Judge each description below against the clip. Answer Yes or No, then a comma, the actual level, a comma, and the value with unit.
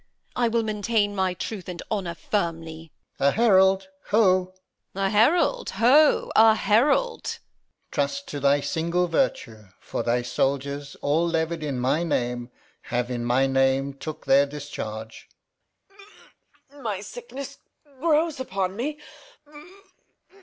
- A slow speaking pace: Yes, slow, 130 wpm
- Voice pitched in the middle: Yes, medium, 180 Hz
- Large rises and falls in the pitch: Yes, wide, 8.1 semitones